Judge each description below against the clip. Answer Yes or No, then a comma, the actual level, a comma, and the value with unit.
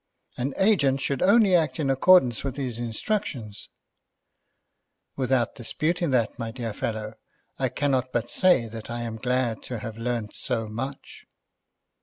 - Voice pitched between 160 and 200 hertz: No, low, 125 Hz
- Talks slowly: No, average, 145 wpm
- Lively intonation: No, average, 3.5 semitones